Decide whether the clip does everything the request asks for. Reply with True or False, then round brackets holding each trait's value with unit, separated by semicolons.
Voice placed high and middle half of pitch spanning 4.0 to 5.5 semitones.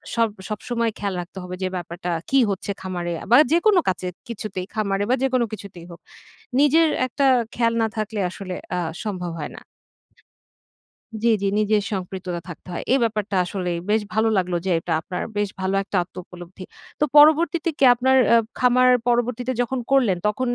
True (210 Hz; 5.1 semitones)